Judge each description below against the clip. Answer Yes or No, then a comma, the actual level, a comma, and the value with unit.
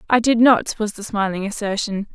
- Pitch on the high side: Yes, high, 215 Hz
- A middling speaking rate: Yes, average, 195 wpm